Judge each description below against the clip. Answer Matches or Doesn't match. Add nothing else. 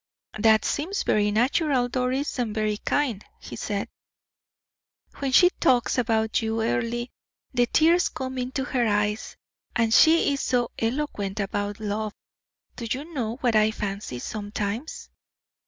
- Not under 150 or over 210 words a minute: Doesn't match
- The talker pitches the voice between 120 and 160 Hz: Doesn't match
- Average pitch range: Matches